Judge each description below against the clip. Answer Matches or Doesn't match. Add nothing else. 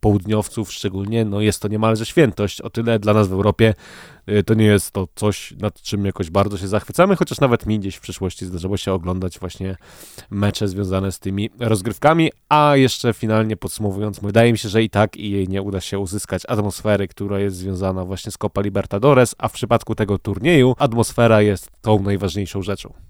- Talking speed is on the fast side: Matches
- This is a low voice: Matches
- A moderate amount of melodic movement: Doesn't match